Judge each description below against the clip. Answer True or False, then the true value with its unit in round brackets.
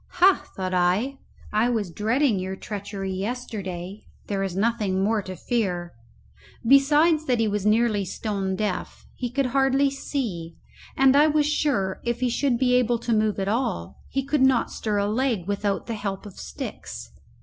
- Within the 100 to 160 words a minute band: False (170 wpm)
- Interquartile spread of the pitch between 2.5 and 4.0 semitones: False (5.2 semitones)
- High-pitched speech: True (220 Hz)